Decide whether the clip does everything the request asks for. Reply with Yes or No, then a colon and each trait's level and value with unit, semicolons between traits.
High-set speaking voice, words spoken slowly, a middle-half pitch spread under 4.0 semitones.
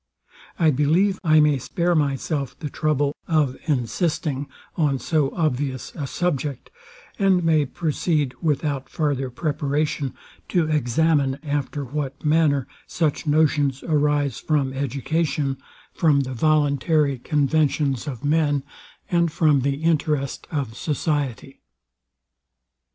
No: medium, 145 Hz; slow, 110 wpm; narrow, 2.4 semitones